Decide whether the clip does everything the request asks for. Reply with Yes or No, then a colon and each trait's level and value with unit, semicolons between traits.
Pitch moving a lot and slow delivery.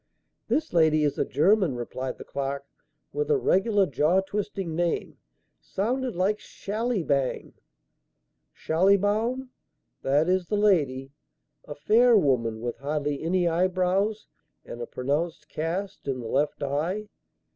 Yes: wide, 6.3 semitones; slow, 125 wpm